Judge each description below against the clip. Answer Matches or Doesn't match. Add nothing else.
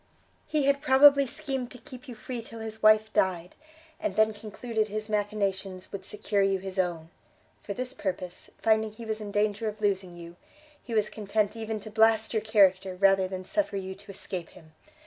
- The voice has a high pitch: Matches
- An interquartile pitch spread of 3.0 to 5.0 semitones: Doesn't match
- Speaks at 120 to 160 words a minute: Doesn't match